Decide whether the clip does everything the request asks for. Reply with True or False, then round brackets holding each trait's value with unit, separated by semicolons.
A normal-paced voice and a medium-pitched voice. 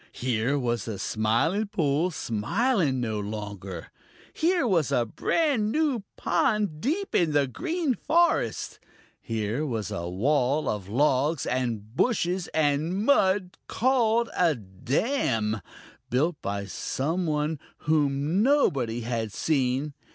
False (120 wpm; 145 Hz)